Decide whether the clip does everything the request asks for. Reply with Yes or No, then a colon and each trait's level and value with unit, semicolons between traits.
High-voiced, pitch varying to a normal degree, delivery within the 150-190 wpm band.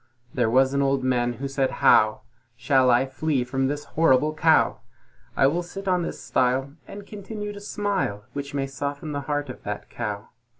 No: medium, 140 Hz; average, 3.6 semitones; average, 185 wpm